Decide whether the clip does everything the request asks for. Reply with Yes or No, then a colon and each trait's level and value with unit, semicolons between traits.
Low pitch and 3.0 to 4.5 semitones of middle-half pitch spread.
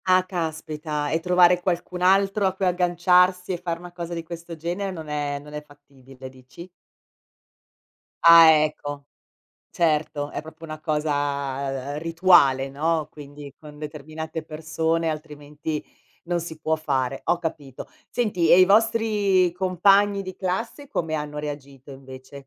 No: medium, 160 Hz; average, 3.4 semitones